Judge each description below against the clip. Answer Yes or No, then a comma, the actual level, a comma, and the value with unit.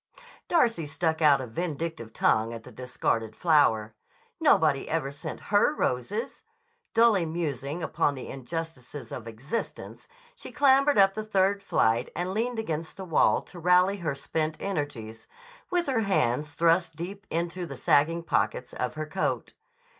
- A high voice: No, medium, 165 Hz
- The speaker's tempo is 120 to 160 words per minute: Yes, average, 150 wpm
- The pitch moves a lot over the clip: Yes, wide, 6.1 semitones